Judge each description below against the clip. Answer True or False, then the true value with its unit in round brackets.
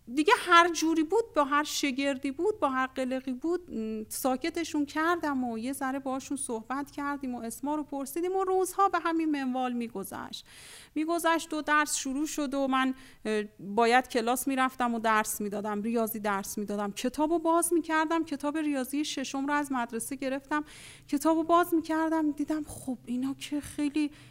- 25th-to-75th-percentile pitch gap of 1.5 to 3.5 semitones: False (3.9 semitones)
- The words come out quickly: True (165 wpm)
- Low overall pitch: False (285 Hz)